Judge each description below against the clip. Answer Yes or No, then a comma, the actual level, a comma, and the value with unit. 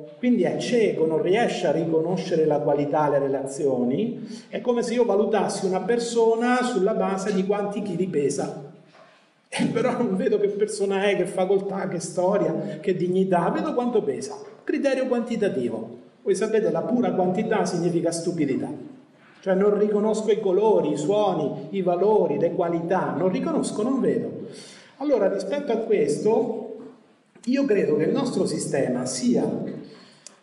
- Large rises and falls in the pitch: No, average, 4.6 semitones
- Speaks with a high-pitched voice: Yes, high, 205 Hz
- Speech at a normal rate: Yes, average, 150 wpm